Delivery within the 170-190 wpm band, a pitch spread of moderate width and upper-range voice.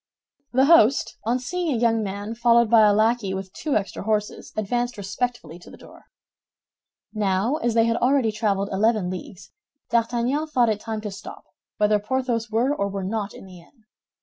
Yes: average, 180 wpm; average, 3.1 semitones; high, 225 Hz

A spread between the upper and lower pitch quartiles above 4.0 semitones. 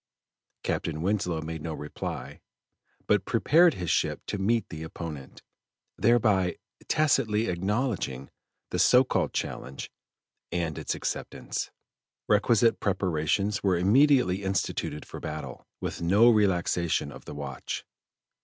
Yes: average, 5.3 semitones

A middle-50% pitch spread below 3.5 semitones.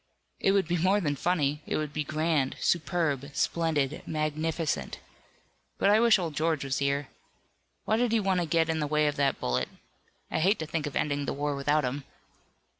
Yes: average, 3.1 semitones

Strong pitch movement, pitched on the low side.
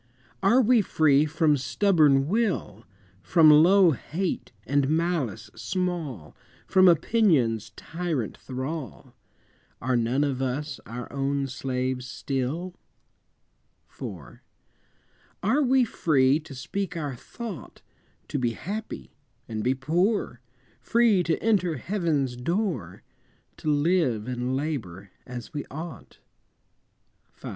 No: wide, 5.8 semitones; medium, 145 Hz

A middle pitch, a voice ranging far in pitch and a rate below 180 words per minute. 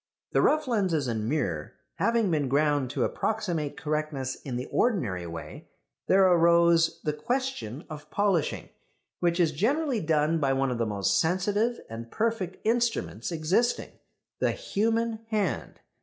Yes: medium, 165 Hz; wide, 7.8 semitones; average, 140 wpm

